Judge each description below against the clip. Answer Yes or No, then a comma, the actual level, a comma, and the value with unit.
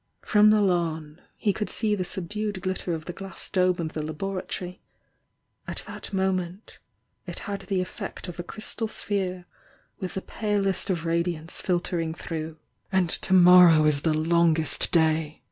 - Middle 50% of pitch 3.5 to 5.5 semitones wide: No, average, 3.0 semitones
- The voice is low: No, medium, 180 Hz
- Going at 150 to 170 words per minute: Yes, average, 160 wpm